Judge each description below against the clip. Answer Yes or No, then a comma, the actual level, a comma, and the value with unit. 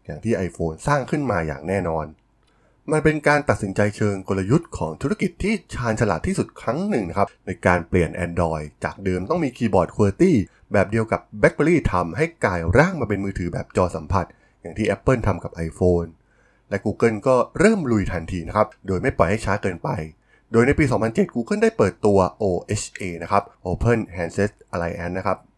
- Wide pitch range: Yes, wide, 5.8 semitones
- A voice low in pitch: Yes, low, 100 Hz